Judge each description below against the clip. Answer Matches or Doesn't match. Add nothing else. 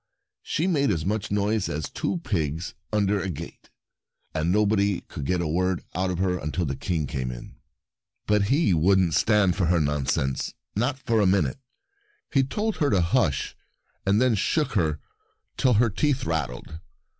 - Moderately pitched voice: Doesn't match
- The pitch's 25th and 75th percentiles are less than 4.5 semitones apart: Doesn't match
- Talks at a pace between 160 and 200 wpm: Matches